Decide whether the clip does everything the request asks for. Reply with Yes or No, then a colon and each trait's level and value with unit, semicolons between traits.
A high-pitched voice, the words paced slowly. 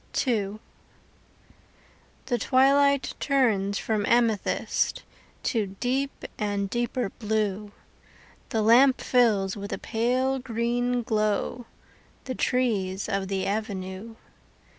Yes: high, 225 Hz; slow, 95 wpm